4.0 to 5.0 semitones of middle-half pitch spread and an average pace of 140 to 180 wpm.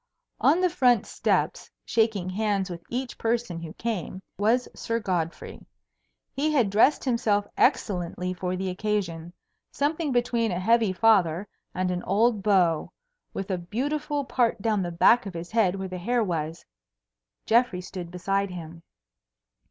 Yes: average, 4.4 semitones; average, 150 wpm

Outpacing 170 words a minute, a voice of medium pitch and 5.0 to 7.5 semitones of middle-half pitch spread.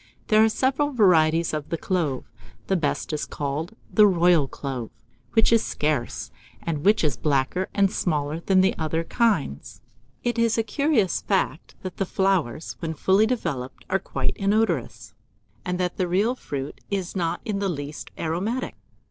No: average, 165 wpm; medium, 180 Hz; wide, 5.4 semitones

